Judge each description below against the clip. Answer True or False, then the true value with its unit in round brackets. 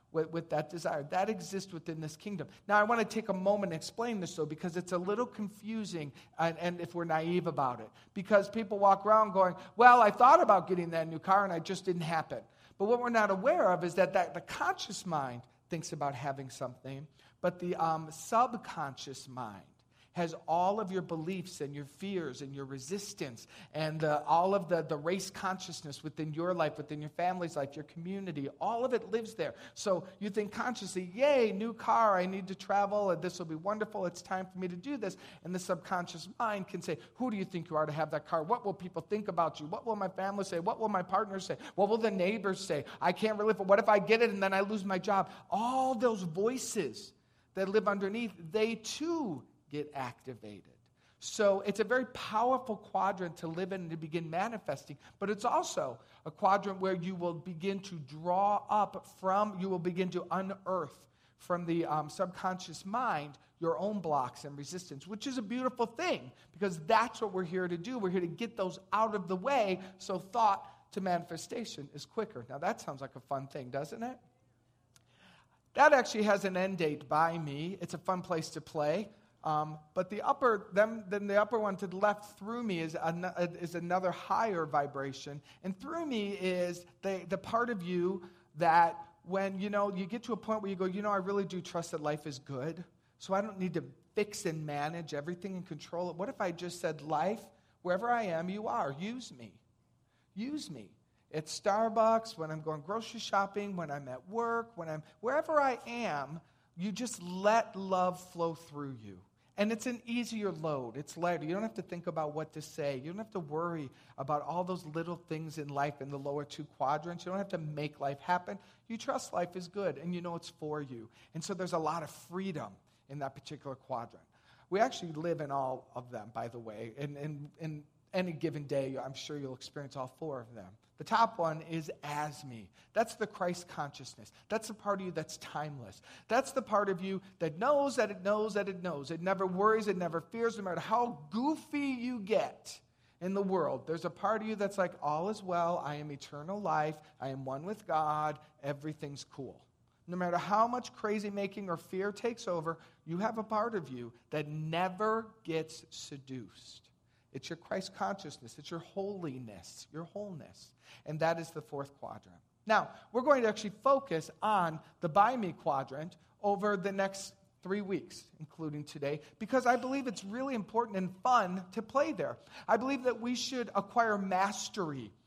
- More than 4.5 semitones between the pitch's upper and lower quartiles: True (5.1 semitones)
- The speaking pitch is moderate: True (180 Hz)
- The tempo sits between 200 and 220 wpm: True (205 wpm)